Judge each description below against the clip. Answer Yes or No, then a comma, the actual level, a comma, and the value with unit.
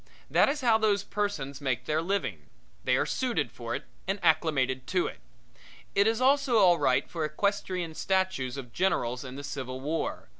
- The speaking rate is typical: Yes, average, 180 wpm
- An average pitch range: No, wide, 7.3 semitones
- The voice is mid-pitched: Yes, medium, 160 Hz